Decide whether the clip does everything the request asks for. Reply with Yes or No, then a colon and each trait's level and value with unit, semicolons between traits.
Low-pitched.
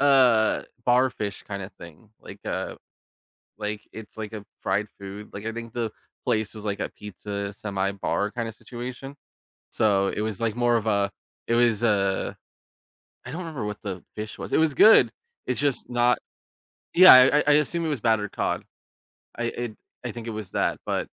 Yes: low, 110 Hz